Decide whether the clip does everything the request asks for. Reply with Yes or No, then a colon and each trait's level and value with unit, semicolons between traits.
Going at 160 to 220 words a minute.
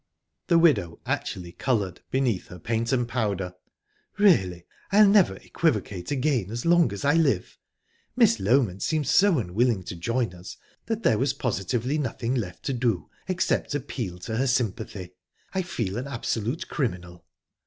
No: average, 150 wpm